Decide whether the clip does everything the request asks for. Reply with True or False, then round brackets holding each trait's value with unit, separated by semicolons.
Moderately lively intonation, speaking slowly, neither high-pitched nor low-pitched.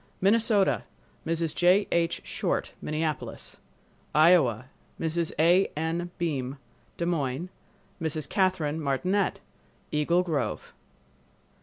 True (3.0 semitones; 85 wpm; 165 Hz)